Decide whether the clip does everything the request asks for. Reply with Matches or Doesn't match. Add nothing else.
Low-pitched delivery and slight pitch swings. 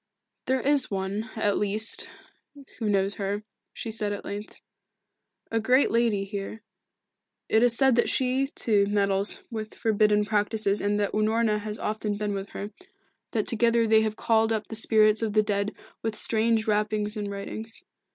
Doesn't match